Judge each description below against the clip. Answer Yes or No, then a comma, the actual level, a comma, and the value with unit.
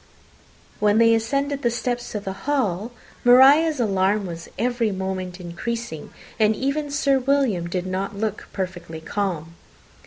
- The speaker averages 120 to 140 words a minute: Yes, slow, 135 wpm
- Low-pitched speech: No, high, 215 Hz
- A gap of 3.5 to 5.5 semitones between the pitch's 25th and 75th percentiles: Yes, average, 5.1 semitones